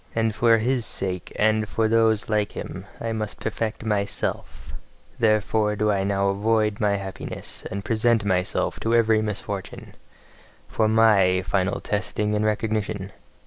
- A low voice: Yes, low, 105 Hz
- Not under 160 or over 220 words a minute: No, average, 145 wpm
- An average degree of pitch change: No, narrow, 1.8 semitones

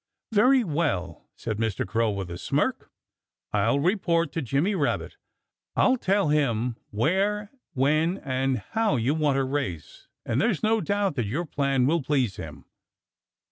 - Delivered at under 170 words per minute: Yes, average, 150 wpm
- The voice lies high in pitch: No, medium, 145 Hz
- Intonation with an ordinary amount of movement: No, wide, 8.1 semitones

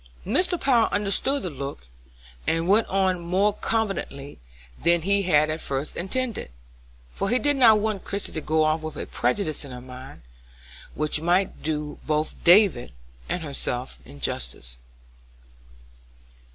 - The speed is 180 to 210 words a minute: No, average, 140 wpm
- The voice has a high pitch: No, medium, 170 Hz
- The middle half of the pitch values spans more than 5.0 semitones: Yes, wide, 5.6 semitones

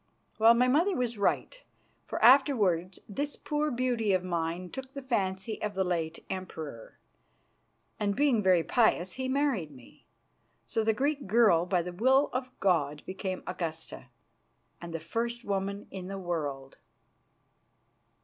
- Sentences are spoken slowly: No, average, 145 wpm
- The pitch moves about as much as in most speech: No, wide, 6.1 semitones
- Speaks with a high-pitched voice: Yes, high, 200 Hz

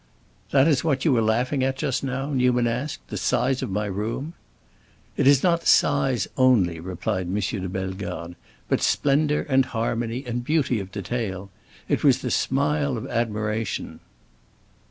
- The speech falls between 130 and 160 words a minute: Yes, average, 155 wpm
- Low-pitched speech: Yes, low, 120 Hz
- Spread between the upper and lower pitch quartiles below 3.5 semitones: No, average, 4.7 semitones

